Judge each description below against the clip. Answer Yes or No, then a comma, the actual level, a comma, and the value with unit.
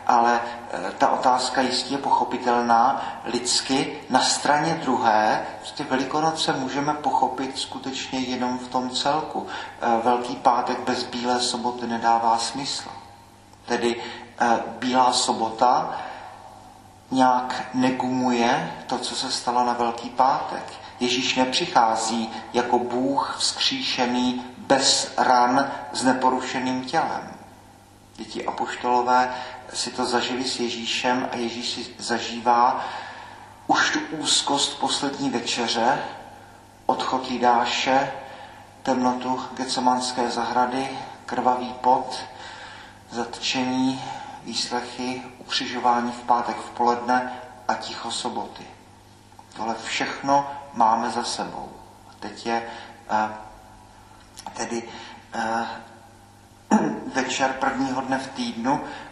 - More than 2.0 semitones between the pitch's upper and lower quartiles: No, narrow, 1.6 semitones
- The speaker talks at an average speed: No, slow, 95 wpm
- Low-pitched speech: Yes, low, 125 Hz